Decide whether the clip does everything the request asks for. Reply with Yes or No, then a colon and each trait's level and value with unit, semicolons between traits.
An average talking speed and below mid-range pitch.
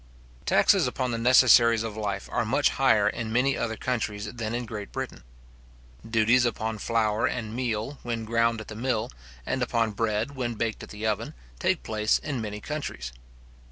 Yes: average, 175 wpm; low, 115 Hz